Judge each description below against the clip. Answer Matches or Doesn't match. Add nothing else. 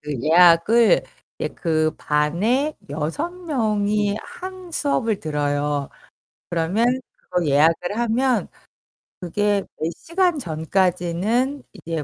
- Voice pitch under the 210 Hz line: Matches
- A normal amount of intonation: Doesn't match